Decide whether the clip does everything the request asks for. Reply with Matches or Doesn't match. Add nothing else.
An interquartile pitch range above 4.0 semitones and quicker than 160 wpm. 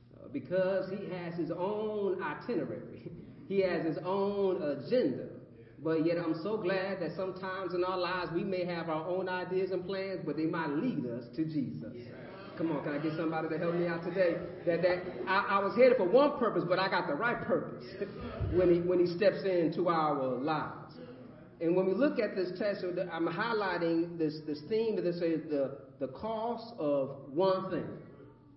Doesn't match